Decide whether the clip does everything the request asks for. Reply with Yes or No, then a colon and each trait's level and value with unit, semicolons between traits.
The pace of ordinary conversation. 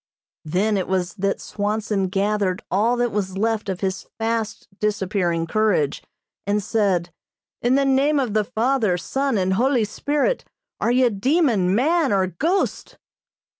Yes: average, 145 wpm